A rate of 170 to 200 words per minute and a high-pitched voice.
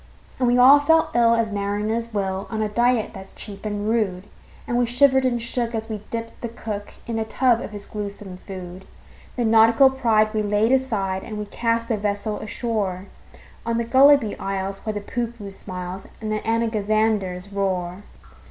Yes: average, 180 wpm; high, 215 Hz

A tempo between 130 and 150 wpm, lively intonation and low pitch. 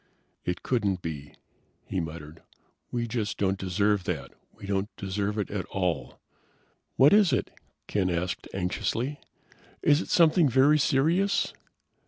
Yes: slow, 135 wpm; wide, 6.4 semitones; low, 105 Hz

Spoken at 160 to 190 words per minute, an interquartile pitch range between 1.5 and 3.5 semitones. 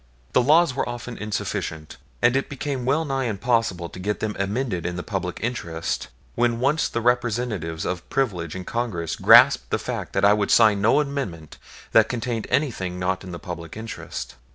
No: average, 180 wpm; wide, 5.5 semitones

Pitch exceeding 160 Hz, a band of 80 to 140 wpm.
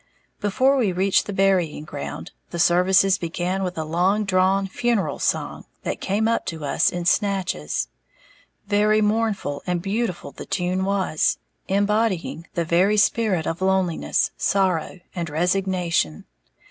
Yes: high, 190 Hz; slow, 135 wpm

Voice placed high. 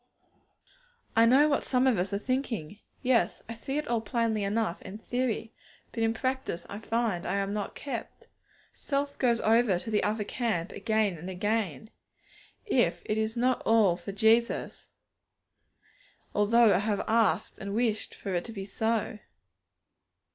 Yes: high, 220 Hz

